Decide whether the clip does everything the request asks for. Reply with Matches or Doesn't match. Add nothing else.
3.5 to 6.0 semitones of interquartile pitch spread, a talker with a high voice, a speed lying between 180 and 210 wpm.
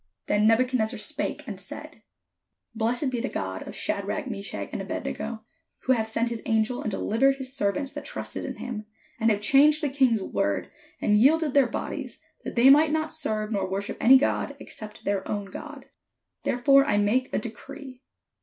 Matches